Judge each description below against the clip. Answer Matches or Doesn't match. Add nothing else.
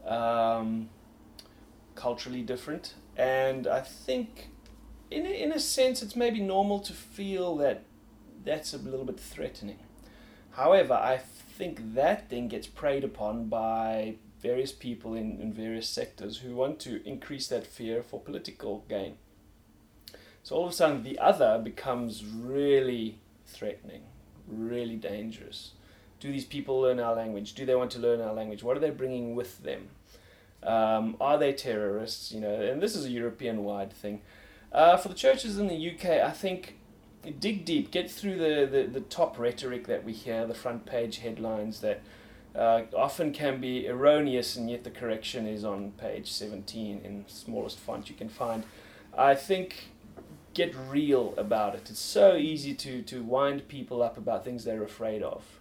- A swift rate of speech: Doesn't match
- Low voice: Matches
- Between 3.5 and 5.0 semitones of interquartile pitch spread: Matches